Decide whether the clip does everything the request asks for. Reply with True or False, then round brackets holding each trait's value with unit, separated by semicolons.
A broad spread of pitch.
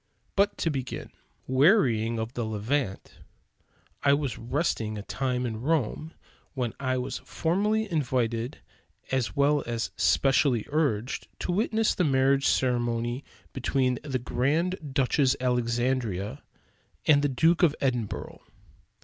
False (3.7 semitones)